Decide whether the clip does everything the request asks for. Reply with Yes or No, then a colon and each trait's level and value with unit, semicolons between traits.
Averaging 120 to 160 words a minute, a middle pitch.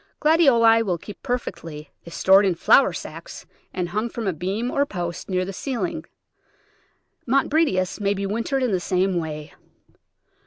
No: average, 155 wpm; high, 200 Hz